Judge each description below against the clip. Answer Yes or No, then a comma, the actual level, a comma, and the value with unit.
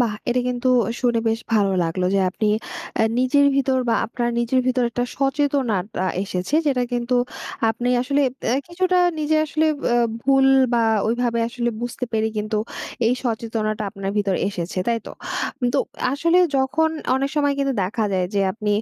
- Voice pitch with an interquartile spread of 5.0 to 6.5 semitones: No, average, 4.0 semitones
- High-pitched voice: Yes, high, 240 Hz